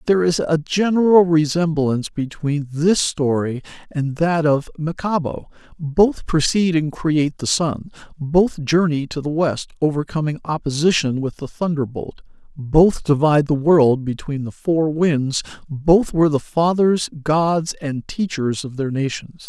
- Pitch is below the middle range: No, medium, 155 Hz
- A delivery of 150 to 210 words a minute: No, average, 140 wpm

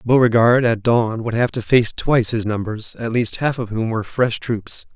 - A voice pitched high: No, low, 115 Hz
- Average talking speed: No, fast, 220 wpm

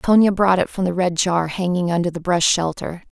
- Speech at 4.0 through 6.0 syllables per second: Yes, 5.3 syllables/s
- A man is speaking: No, female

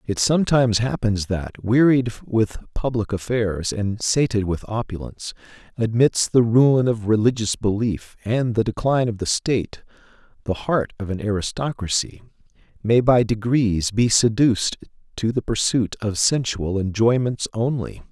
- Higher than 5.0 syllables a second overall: No, 4.6 syllables/s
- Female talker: No, male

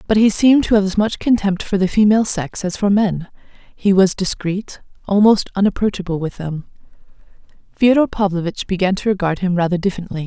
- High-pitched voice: Yes, high, 195 Hz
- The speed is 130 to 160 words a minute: No, average, 175 wpm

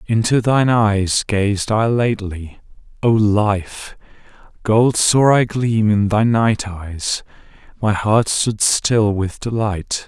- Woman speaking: No, male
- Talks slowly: Yes, slow, 125 wpm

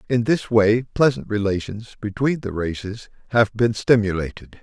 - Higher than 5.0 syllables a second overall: No, 4.7 syllables/s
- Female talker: No, male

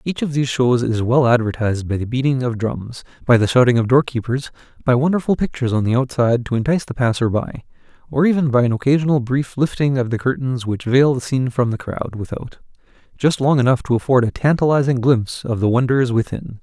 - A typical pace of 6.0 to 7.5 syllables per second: Yes, 6.1 syllables/s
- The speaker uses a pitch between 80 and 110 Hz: No, low, 125 Hz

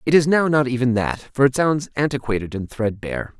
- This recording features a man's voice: Yes, male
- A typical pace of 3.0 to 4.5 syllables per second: No, 5.7 syllables/s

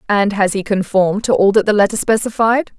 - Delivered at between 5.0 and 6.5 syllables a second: Yes, 5.8 syllables/s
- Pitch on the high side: Yes, high, 205 Hz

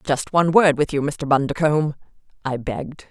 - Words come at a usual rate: Yes, average, 175 wpm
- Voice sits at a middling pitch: Yes, medium, 145 Hz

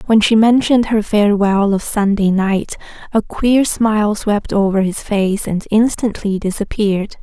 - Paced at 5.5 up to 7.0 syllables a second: No, 4.5 syllables/s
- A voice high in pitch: Yes, high, 210 Hz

